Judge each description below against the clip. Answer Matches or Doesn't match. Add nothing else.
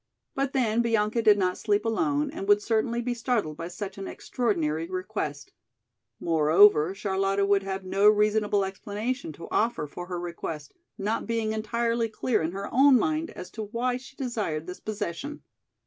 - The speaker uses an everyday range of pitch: Matches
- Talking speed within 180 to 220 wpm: Doesn't match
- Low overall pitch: Doesn't match